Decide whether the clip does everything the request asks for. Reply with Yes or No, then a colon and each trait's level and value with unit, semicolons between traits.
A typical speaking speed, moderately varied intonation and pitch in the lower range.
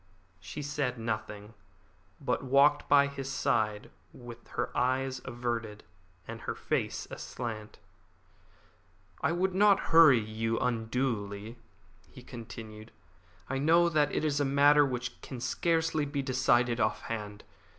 No: slow, 130 wpm; average, 4.1 semitones; low, 125 Hz